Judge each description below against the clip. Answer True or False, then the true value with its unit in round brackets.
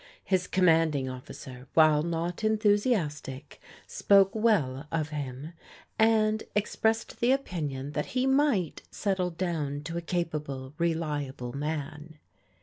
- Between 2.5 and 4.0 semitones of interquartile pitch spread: False (5.5 semitones)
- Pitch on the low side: False (165 Hz)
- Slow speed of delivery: True (130 wpm)